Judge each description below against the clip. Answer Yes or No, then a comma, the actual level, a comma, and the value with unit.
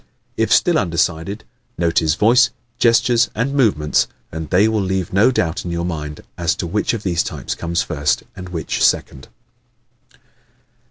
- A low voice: Yes, very low, 90 Hz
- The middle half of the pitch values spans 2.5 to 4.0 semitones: No, average, 5.1 semitones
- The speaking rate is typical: Yes, average, 160 wpm